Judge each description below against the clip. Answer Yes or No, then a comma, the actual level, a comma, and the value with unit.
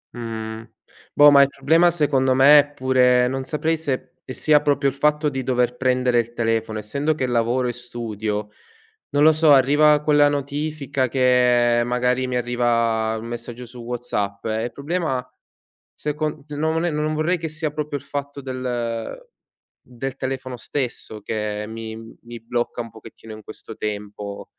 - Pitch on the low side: Yes, low, 125 Hz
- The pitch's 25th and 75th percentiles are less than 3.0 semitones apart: No, average, 3.7 semitones